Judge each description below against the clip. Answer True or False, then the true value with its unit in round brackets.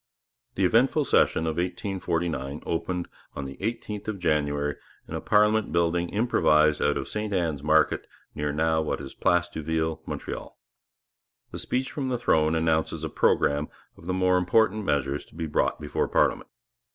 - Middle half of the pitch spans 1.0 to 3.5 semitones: False (4.6 semitones)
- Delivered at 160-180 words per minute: True (165 wpm)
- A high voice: False (85 Hz)